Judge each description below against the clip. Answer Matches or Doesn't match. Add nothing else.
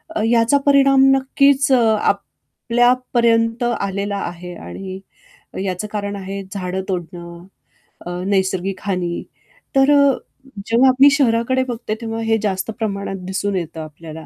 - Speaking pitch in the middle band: Doesn't match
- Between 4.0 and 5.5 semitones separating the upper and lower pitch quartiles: Matches